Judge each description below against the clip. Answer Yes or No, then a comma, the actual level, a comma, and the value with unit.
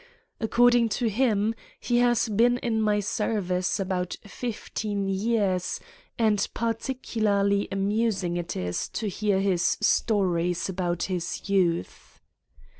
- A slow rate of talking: Yes, slow, 115 wpm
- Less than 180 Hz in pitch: No, high, 205 Hz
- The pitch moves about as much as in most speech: Yes, average, 3.4 semitones